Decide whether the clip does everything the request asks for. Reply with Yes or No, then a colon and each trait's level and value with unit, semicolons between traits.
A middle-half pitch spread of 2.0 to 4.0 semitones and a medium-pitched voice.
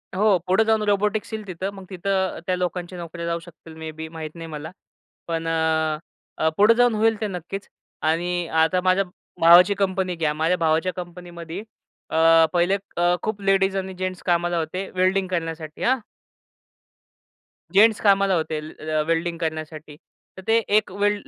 Yes: average, 3.1 semitones; medium, 175 Hz